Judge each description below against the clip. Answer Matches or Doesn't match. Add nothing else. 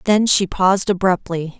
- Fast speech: Doesn't match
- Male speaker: Doesn't match